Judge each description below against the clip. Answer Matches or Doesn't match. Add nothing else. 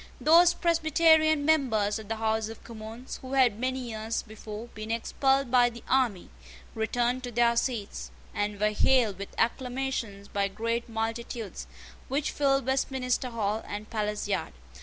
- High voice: Matches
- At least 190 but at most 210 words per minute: Doesn't match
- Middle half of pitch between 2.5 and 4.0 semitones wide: Matches